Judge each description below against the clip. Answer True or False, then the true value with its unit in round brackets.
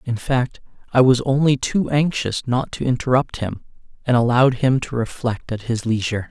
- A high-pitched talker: False (125 Hz)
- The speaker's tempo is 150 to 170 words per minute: False (180 wpm)